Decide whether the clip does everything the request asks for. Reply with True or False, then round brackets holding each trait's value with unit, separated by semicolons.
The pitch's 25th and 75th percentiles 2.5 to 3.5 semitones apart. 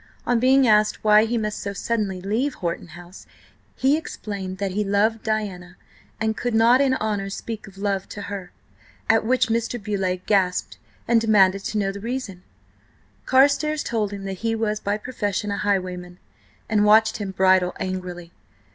True (2.8 semitones)